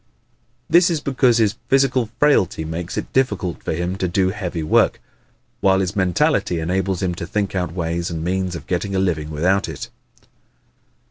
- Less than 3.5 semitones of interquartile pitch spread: Yes, average, 3.1 semitones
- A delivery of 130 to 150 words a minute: No, average, 175 wpm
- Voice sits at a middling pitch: No, very low, 95 Hz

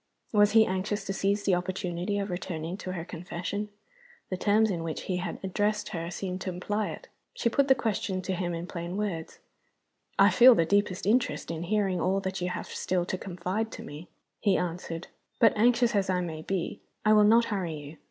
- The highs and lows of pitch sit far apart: No, average, 2.9 semitones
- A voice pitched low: No, high, 190 Hz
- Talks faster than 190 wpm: Yes, fast, 205 wpm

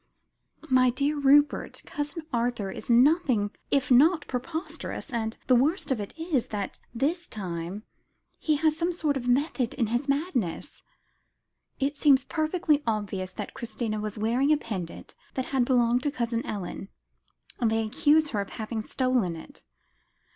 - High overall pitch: Yes, very high, 250 Hz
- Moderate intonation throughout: Yes, average, 4.9 semitones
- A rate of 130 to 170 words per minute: Yes, average, 155 wpm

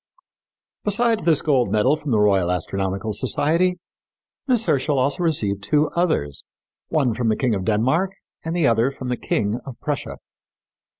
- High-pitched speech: No, low, 130 Hz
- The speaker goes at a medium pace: Yes, average, 165 wpm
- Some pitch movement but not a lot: No, wide, 7.1 semitones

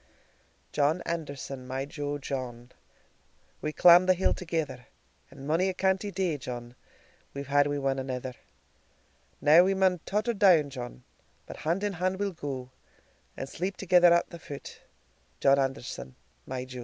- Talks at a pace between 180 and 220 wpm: No, average, 155 wpm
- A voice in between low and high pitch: Yes, medium, 145 Hz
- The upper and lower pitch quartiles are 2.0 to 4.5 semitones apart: No, average, 5.3 semitones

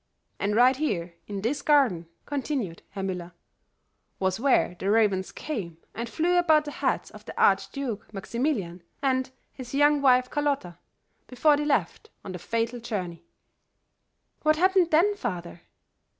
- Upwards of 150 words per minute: No, average, 145 wpm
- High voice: Yes, high, 245 Hz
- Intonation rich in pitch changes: Yes, wide, 7.3 semitones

